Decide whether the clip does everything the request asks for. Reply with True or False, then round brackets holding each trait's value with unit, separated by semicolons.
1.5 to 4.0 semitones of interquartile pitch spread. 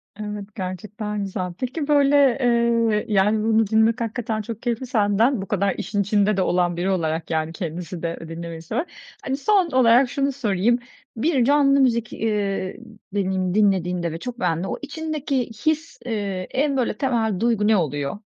False (4.9 semitones)